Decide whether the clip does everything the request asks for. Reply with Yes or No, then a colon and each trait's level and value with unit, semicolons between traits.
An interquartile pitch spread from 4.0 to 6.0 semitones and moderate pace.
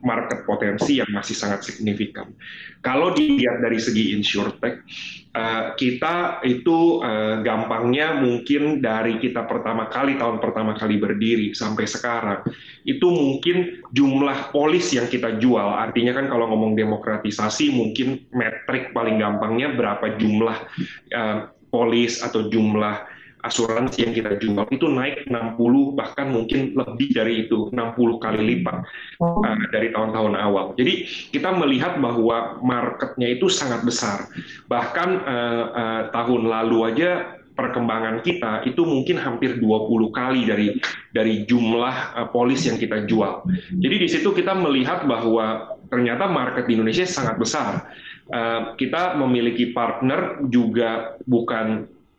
No: average, 2.9 semitones; average, 130 wpm